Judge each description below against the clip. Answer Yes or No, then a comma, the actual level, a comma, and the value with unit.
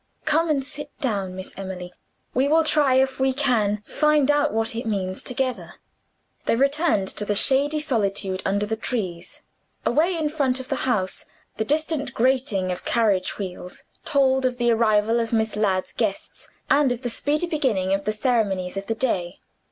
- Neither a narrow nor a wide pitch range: No, wide, 5.7 semitones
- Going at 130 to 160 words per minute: No, average, 175 wpm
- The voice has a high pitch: Yes, high, 235 Hz